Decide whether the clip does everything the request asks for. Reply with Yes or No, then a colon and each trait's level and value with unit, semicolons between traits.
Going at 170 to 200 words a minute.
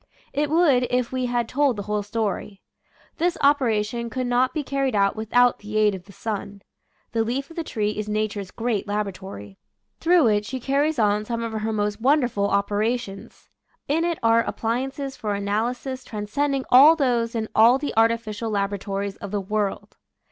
Yes: average, 180 wpm